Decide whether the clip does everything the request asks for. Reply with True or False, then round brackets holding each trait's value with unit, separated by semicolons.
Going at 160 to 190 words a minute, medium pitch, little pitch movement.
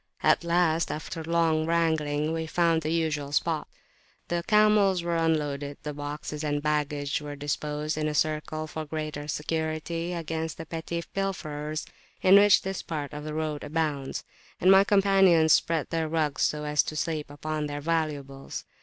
True (165 wpm; 155 Hz; 2.0 semitones)